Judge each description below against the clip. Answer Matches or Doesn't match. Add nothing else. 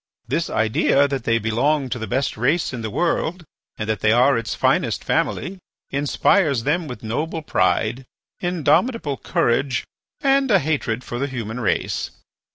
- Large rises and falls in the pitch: Matches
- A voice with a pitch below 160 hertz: Matches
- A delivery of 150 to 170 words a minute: Matches